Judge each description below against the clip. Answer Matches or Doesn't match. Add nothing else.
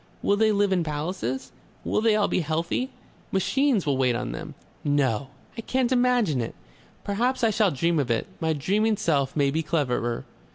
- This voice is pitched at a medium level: Matches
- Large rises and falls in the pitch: Matches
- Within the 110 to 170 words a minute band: Doesn't match